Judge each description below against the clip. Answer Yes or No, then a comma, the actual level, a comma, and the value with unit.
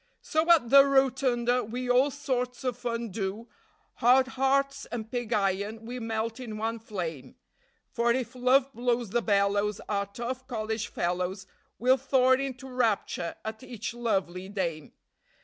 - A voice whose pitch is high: Yes, high, 235 Hz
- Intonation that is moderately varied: Yes, average, 3.4 semitones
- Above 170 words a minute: No, average, 150 wpm